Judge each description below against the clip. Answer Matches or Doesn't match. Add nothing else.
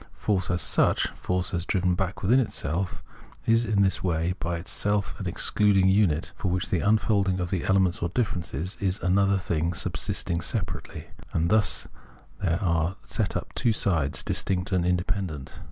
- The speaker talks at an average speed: Matches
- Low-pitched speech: Matches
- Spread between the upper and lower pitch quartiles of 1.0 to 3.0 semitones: Matches